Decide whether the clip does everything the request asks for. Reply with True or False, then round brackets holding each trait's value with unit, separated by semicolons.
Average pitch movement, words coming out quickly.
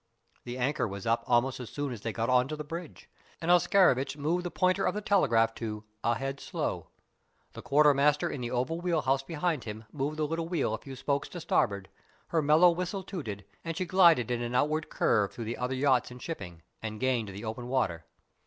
False (5.7 semitones; 210 wpm)